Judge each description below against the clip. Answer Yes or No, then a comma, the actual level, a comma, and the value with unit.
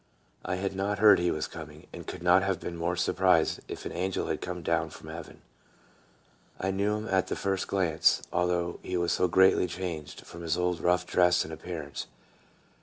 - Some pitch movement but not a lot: No, narrow, 1.8 semitones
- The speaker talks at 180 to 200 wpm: Yes, average, 195 wpm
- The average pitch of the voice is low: Yes, very low, 90 Hz